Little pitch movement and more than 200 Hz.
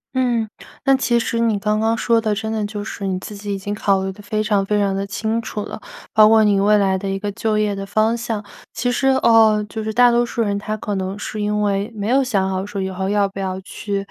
Yes: narrow, 2.0 semitones; high, 210 Hz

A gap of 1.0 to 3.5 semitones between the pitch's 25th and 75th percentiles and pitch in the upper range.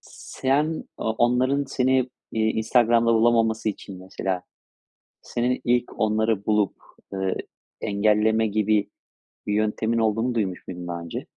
No: narrow, 2.6 semitones; low, 110 Hz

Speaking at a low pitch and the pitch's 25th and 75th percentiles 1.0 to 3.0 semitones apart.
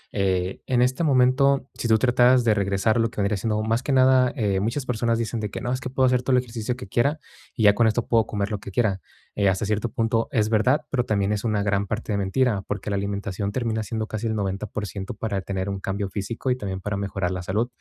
No: low, 110 Hz; average, 3.6 semitones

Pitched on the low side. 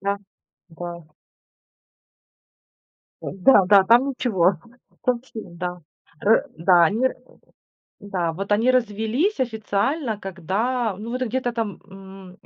No: high, 205 Hz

